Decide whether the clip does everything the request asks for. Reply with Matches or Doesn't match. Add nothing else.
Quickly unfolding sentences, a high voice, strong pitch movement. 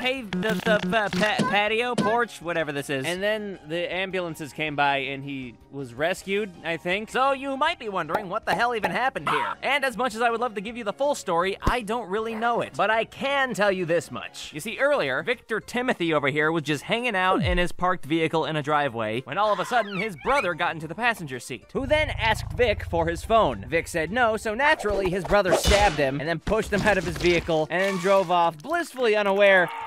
Matches